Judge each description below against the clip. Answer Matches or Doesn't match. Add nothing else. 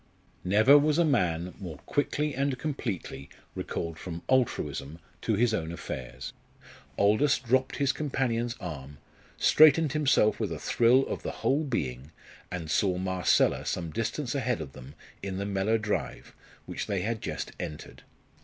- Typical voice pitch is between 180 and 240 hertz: Doesn't match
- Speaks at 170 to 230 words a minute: Doesn't match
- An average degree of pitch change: Doesn't match